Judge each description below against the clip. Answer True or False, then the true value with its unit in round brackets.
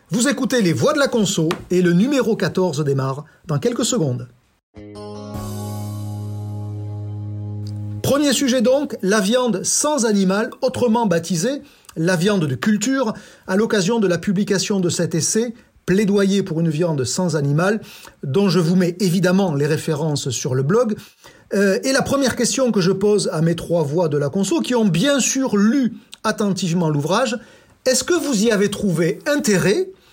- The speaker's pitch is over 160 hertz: True (190 Hz)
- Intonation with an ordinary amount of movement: False (6.8 semitones)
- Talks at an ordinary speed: True (160 wpm)